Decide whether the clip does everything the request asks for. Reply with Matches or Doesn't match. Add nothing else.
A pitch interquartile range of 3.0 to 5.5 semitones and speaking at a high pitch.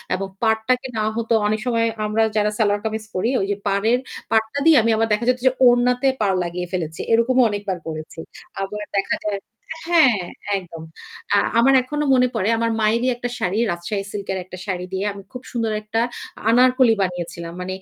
Matches